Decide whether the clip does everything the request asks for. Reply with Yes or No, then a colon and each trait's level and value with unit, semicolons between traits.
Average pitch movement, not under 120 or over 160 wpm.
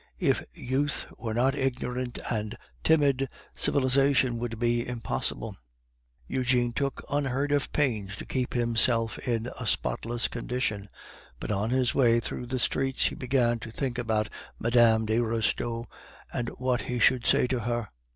No: narrow, 2.2 semitones; average, 150 wpm